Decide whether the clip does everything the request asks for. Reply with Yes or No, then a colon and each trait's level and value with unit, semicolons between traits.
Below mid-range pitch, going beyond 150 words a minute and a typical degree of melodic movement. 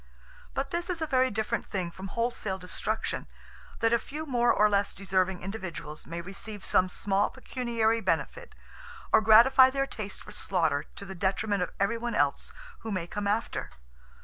No: high, 210 Hz; average, 170 wpm; average, 3.9 semitones